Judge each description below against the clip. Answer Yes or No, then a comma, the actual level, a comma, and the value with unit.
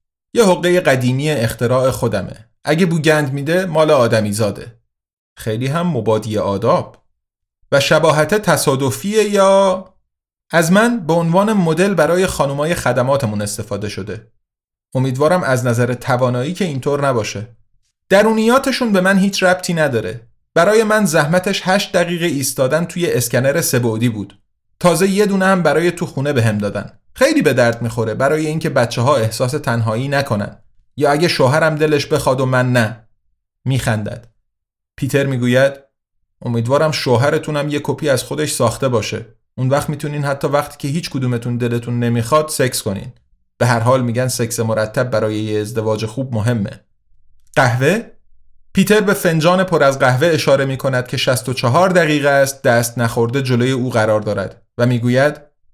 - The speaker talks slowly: No, average, 145 wpm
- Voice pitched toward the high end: No, low, 135 Hz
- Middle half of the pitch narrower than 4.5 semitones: No, wide, 5.6 semitones